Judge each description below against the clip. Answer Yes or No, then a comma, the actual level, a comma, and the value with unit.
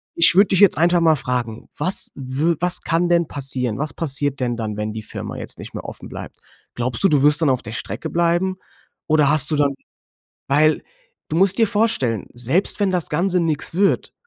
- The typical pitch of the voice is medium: Yes, medium, 155 Hz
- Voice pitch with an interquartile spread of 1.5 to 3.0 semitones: No, average, 5.1 semitones